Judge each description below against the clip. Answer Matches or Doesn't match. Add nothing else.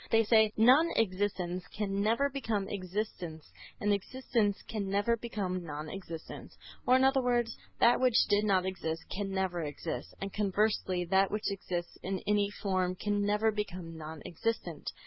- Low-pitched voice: Doesn't match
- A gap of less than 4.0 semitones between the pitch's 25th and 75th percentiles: Matches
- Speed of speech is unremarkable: Matches